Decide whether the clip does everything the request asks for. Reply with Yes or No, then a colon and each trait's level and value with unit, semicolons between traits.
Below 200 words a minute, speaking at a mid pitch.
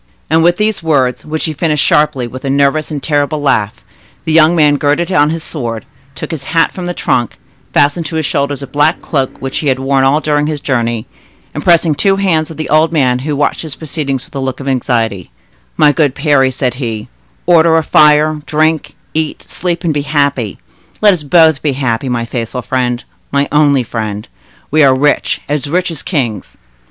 No: fast, 205 wpm; medium, 145 Hz